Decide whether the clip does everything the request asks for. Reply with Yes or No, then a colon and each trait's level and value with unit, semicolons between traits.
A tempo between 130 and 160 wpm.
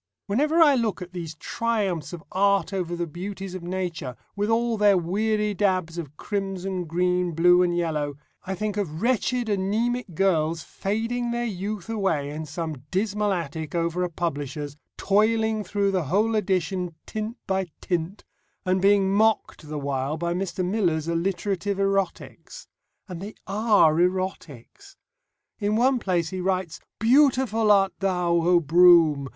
Yes: average, 150 wpm